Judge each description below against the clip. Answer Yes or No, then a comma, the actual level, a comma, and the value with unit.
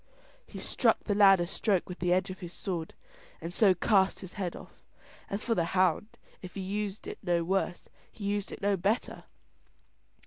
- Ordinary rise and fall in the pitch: No, narrow, 2.3 semitones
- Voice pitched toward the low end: No, high, 190 Hz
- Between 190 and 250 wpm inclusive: Yes, average, 195 wpm